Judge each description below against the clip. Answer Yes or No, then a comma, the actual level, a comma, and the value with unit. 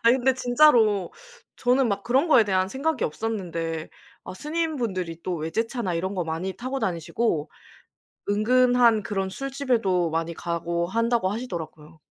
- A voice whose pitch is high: Yes, high, 205 Hz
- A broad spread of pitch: Yes, wide, 6.3 semitones